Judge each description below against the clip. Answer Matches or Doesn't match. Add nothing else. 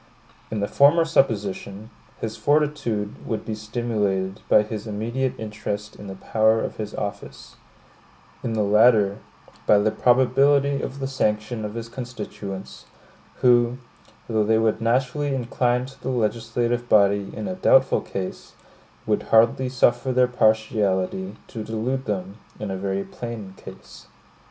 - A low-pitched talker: Matches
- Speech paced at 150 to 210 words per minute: Doesn't match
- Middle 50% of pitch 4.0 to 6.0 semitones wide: Doesn't match